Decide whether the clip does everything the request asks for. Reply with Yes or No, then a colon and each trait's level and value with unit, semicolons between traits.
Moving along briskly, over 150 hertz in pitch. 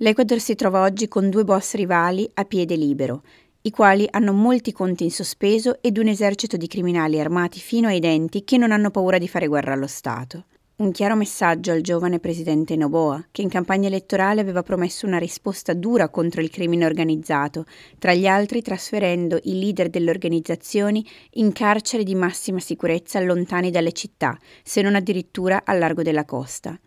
Yes: fast, 175 wpm; medium, 185 Hz